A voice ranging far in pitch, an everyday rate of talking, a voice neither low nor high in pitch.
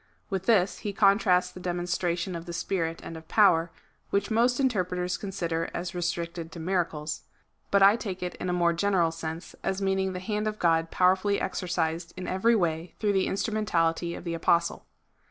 No: average, 2.7 semitones; average, 180 wpm; medium, 180 Hz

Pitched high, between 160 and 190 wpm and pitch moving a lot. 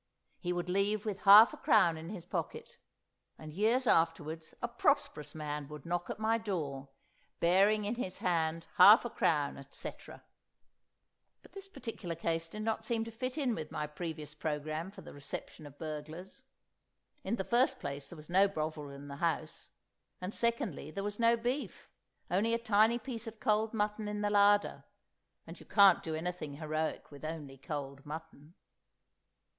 No: medium, 180 Hz; average, 170 wpm; wide, 5.9 semitones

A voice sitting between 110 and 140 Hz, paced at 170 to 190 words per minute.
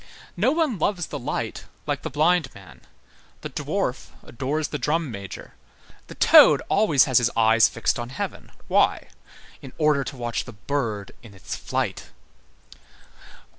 No: low, 135 Hz; average, 150 wpm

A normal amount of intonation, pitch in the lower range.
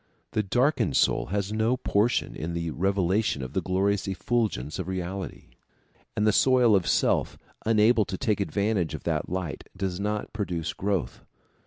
Yes: average, 3.0 semitones; low, 100 Hz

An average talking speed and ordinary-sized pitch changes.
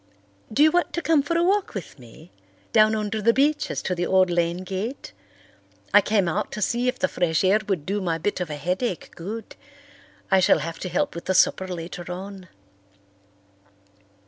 Yes: average, 190 wpm; average, 4.2 semitones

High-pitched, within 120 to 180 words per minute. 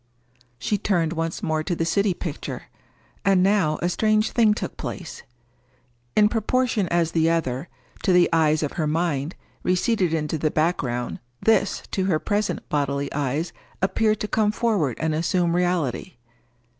No: medium, 170 Hz; average, 155 wpm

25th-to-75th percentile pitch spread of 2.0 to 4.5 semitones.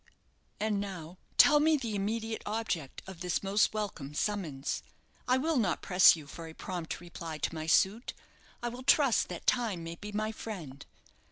No: average, 5.1 semitones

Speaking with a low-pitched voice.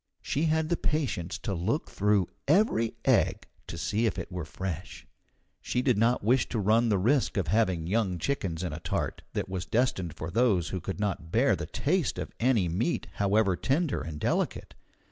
Yes: low, 105 Hz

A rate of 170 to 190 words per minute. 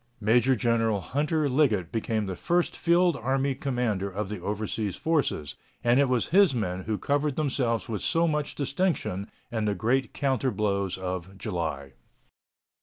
No: average, 155 wpm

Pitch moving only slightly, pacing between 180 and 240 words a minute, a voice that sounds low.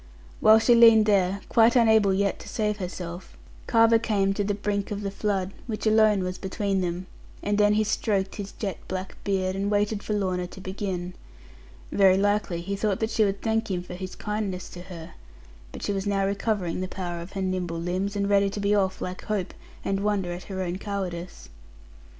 No: narrow, 2.1 semitones; fast, 205 wpm; high, 195 Hz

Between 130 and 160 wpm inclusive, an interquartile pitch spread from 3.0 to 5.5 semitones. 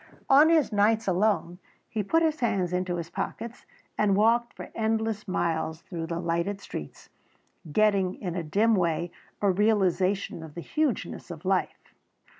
Yes: average, 155 wpm; average, 4.2 semitones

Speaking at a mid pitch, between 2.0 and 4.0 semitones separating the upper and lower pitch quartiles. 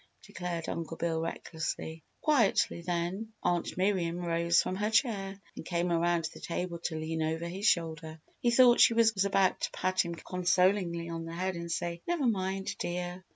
Yes: medium, 175 Hz; narrow, 2.5 semitones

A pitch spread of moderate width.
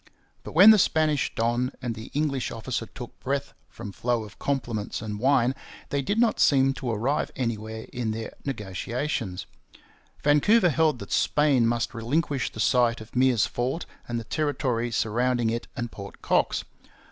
Yes: average, 3.8 semitones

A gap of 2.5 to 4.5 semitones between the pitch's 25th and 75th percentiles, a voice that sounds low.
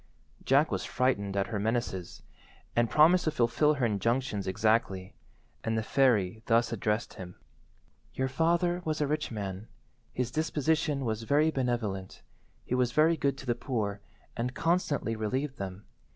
No: wide, 5.4 semitones; low, 120 Hz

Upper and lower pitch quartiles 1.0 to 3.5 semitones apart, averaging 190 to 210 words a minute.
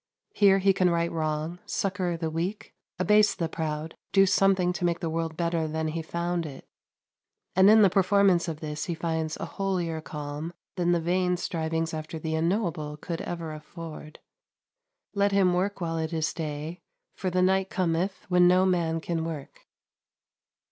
No: narrow, 2.5 semitones; average, 170 wpm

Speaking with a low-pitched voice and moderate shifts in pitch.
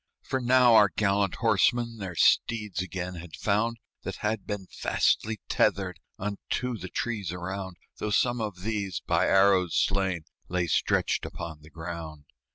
Yes: low, 100 Hz; average, 3.6 semitones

